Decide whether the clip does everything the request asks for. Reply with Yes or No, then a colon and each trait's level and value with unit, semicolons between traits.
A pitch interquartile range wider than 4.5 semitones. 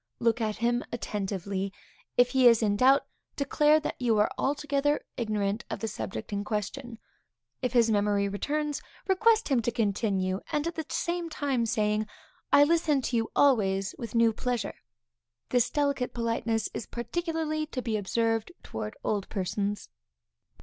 Yes: average, 5.3 semitones